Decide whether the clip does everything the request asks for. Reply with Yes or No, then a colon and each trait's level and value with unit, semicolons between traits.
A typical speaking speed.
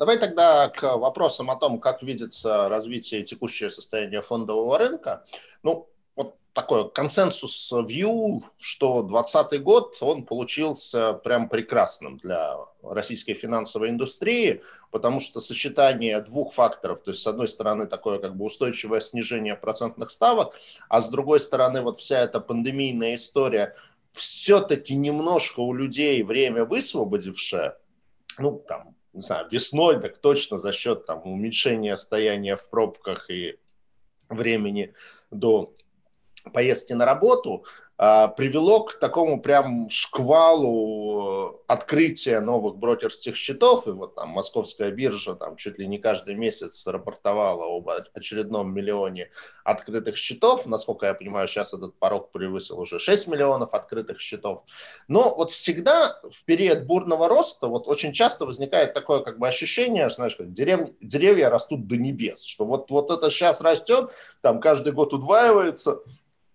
Yes: average, 135 wpm